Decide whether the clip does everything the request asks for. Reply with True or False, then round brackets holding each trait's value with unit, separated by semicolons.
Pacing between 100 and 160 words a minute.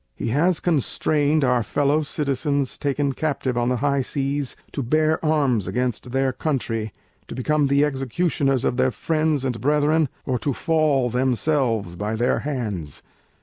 True (150 wpm)